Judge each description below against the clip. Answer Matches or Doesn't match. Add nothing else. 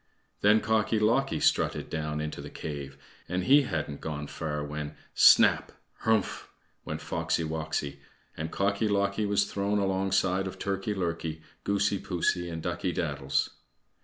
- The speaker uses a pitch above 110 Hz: Doesn't match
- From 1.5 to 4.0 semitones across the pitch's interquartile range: Doesn't match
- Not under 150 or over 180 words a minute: Doesn't match